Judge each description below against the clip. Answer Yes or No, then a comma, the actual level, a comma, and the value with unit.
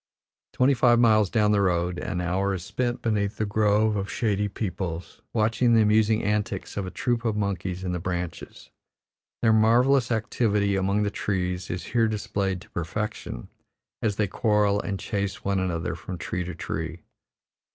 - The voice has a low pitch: Yes, low, 100 Hz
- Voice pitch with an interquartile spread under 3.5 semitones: Yes, average, 3.0 semitones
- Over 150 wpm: Yes, average, 170 wpm